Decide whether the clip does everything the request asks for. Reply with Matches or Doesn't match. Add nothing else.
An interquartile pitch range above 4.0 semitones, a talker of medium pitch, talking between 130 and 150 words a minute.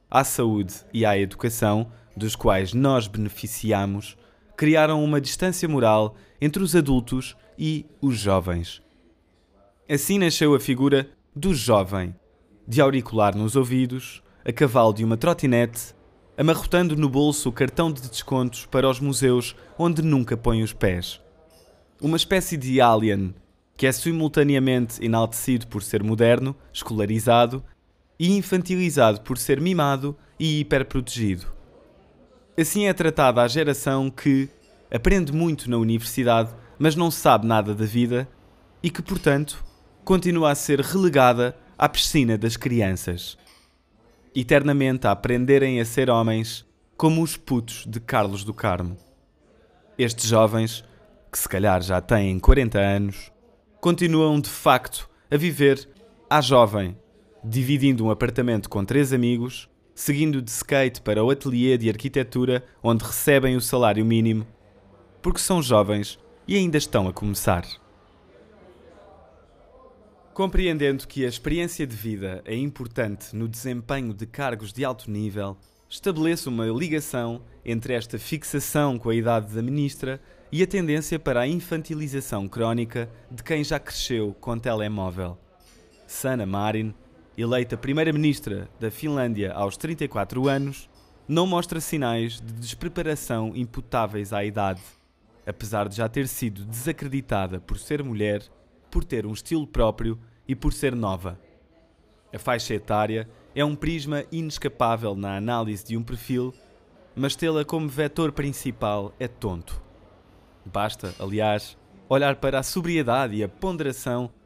Doesn't match